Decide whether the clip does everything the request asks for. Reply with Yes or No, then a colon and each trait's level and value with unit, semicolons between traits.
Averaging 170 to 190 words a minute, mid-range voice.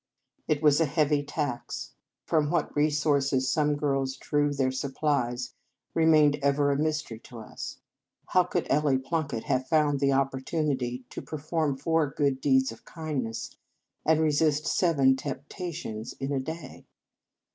No: average, 145 wpm; medium, 145 Hz